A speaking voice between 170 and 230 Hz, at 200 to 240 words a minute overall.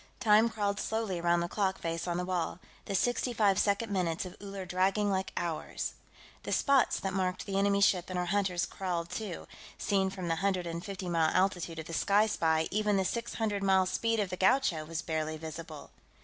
Yes: high, 190 Hz; fast, 205 wpm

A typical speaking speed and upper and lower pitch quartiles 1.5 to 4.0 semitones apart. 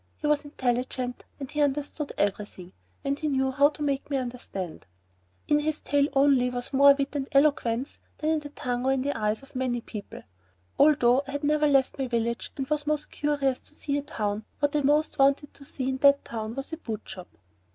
No: fast, 215 wpm; average, 2.8 semitones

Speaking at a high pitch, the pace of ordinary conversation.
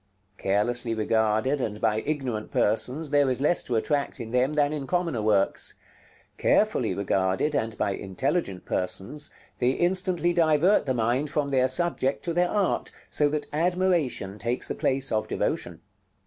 No: low, 130 Hz; average, 155 wpm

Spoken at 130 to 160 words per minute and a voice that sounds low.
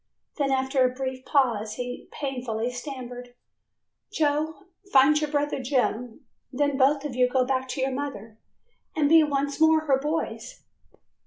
No: average, 150 wpm; very high, 270 Hz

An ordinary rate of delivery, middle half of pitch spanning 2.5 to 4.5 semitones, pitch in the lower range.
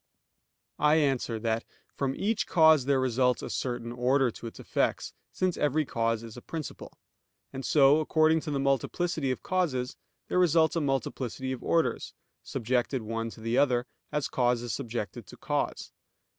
Yes: average, 165 wpm; average, 4.1 semitones; low, 130 Hz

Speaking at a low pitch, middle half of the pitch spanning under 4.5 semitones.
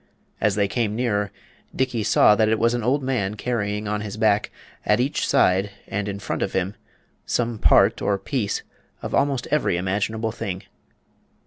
Yes: low, 105 Hz; average, 2.9 semitones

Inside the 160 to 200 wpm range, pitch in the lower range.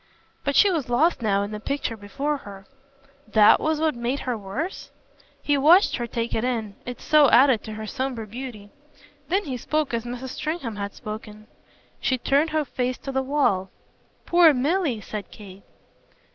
No: average, 175 wpm; very high, 250 Hz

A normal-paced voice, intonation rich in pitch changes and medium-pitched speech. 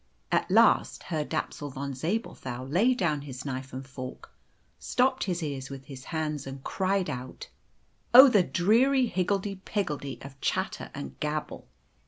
Yes: average, 150 wpm; wide, 6.4 semitones; medium, 150 Hz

